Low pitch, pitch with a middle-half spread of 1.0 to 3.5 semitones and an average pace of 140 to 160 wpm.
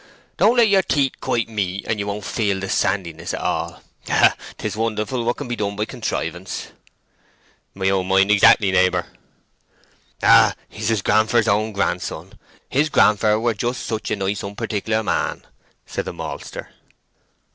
Yes: low, 105 Hz; average, 2.7 semitones; average, 155 wpm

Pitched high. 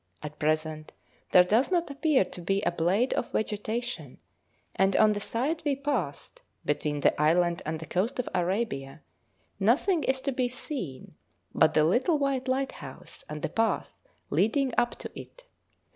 Yes: high, 215 Hz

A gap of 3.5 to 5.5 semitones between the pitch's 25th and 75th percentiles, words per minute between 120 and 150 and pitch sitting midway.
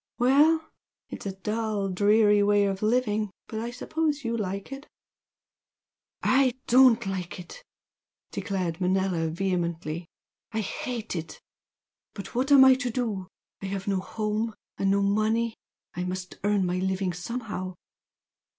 No: average, 3.9 semitones; average, 140 wpm; high, 205 Hz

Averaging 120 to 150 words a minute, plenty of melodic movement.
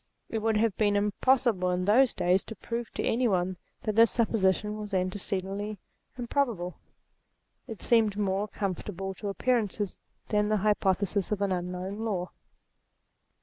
No: average, 145 wpm; average, 2.8 semitones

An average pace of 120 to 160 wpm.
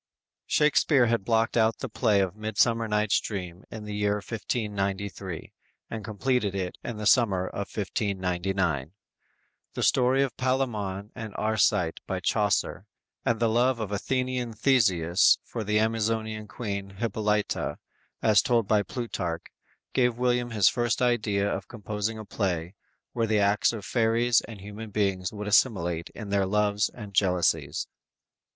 Yes: average, 145 wpm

